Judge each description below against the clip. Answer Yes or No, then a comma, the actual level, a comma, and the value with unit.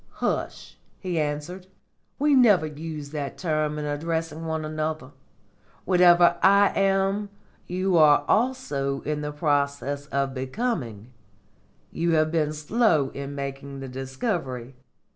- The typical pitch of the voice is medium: Yes, medium, 155 Hz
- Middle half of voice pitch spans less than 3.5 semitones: No, average, 4.2 semitones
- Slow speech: Yes, slow, 120 wpm